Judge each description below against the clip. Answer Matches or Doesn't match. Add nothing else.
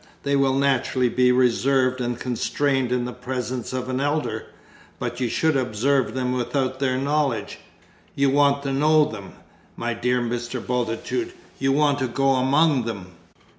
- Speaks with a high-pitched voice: Doesn't match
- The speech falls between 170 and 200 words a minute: Doesn't match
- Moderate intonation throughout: Doesn't match